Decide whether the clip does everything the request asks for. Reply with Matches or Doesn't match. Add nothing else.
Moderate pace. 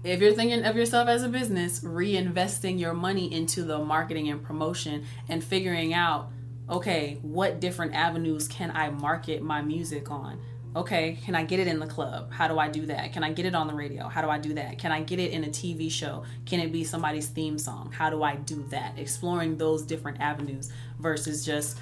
Doesn't match